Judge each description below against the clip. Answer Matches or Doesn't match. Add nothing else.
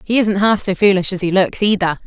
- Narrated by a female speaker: Matches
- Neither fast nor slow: Doesn't match